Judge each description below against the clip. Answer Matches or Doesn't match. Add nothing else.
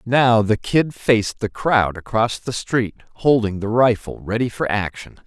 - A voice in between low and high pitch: Doesn't match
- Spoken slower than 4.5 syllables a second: Matches